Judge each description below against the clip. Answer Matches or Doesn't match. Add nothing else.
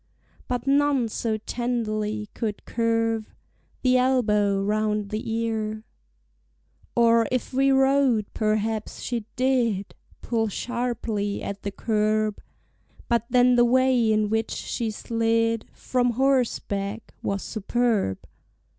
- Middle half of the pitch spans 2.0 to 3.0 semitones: Matches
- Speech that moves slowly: Matches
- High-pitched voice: Matches